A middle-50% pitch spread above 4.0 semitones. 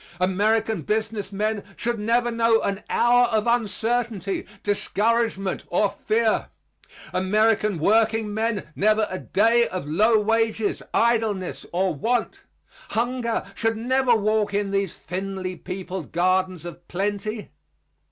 No: average, 2.8 semitones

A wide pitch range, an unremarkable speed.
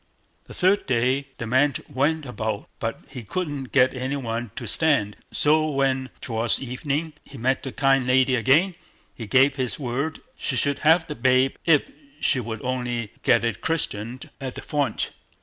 No: average, 3.2 semitones; average, 175 wpm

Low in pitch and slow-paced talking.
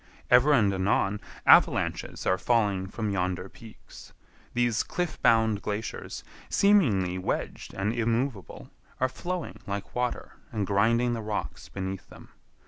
Yes: low, 110 Hz; slow, 130 wpm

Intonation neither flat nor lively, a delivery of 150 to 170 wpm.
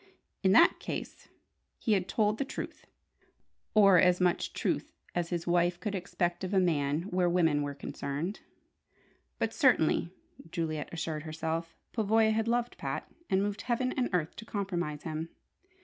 Yes: average, 4.3 semitones; average, 155 wpm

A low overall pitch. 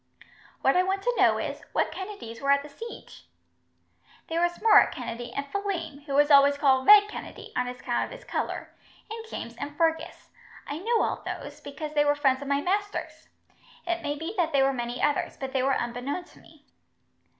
No: very high, 290 Hz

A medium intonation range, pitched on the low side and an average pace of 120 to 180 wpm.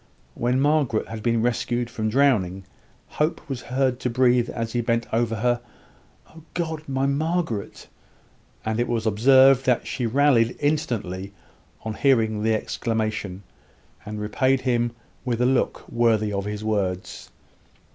Yes: average, 3.4 semitones; low, 120 Hz; average, 145 wpm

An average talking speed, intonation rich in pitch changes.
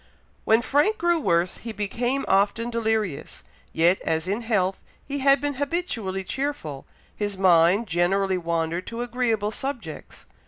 Yes: average, 145 wpm; wide, 5.7 semitones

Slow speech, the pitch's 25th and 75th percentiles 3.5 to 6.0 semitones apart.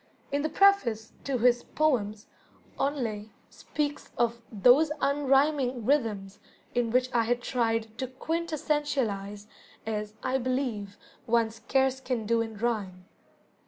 Yes: slow, 125 wpm; average, 3.8 semitones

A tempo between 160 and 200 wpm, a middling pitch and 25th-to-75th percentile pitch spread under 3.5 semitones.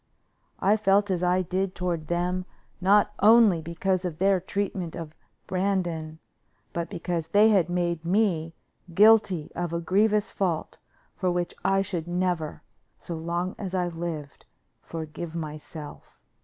No: average, 140 wpm; medium, 180 Hz; average, 2.7 semitones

